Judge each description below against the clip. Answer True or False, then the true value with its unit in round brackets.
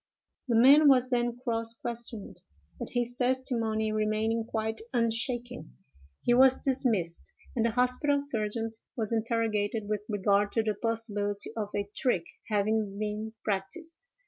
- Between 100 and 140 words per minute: True (135 wpm)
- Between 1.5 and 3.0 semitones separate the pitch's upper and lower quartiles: True (2.5 semitones)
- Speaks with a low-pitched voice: False (225 Hz)